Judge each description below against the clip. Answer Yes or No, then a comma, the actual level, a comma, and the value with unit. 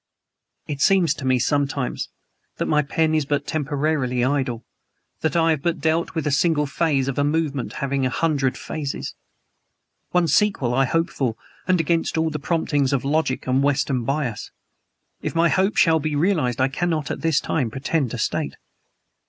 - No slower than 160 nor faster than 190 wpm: Yes, average, 175 wpm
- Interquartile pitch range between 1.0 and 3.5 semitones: Yes, average, 3.2 semitones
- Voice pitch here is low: No, medium, 145 Hz